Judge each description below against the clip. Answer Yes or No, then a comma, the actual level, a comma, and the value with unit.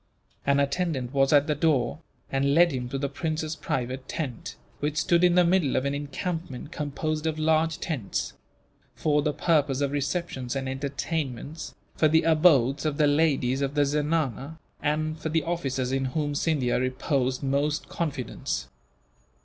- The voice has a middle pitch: Yes, medium, 145 Hz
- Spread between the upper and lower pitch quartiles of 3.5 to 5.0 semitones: No, average, 2.8 semitones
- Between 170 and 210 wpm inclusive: No, average, 160 wpm